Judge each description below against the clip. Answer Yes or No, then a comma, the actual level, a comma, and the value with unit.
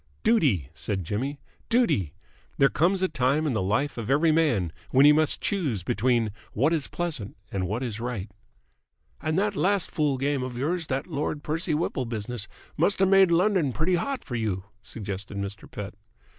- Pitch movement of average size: No, wide, 7.3 semitones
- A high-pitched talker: No, low, 135 Hz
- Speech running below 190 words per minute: Yes, average, 180 wpm